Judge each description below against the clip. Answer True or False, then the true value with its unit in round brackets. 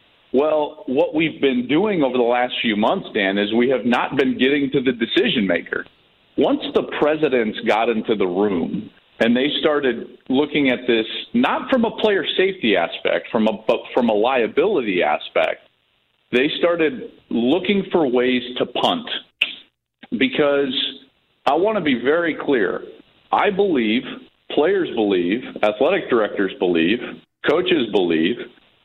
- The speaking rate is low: False (145 wpm)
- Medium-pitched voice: True (145 Hz)